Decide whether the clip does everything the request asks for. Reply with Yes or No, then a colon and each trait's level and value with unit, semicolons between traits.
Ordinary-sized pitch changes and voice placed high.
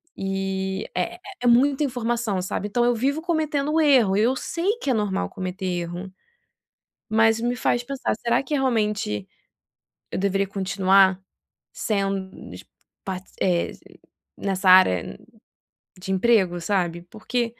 Yes: average, 4.4 semitones; high, 205 Hz